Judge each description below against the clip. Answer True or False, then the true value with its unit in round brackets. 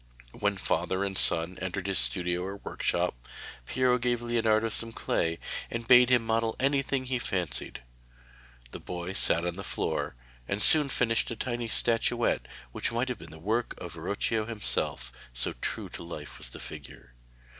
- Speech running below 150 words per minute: False (170 wpm)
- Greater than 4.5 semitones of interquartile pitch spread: True (5.1 semitones)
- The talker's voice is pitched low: True (110 Hz)